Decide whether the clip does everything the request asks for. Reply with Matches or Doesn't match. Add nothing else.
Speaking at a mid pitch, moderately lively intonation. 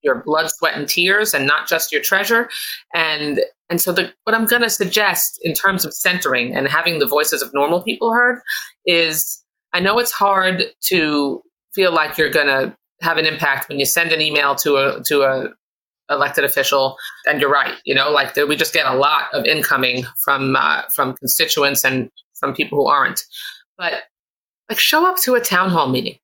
Doesn't match